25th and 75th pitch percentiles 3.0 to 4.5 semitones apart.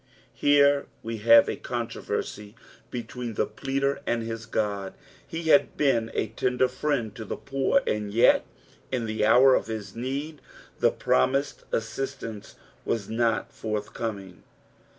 Yes: average, 3.6 semitones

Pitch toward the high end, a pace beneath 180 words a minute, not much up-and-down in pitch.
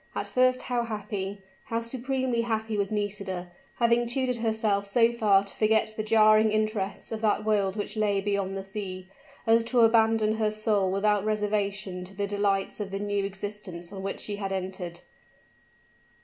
Yes: high, 210 Hz; average, 170 wpm; narrow, 2.2 semitones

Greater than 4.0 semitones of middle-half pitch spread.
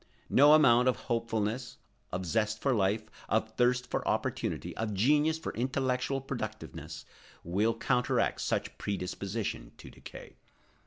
No: average, 3.3 semitones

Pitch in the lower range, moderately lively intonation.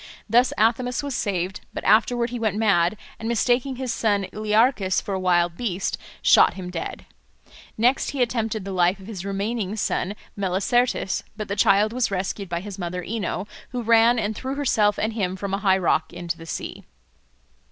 No: high, 205 Hz; average, 3.6 semitones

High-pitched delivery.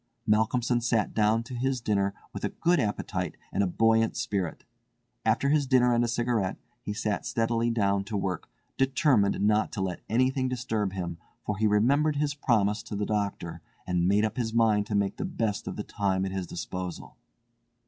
No: low, 110 Hz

